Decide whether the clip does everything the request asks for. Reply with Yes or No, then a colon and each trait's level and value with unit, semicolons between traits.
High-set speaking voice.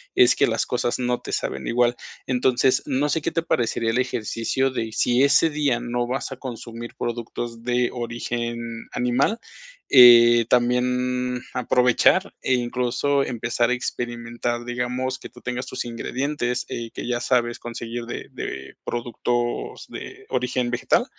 No: low, 120 Hz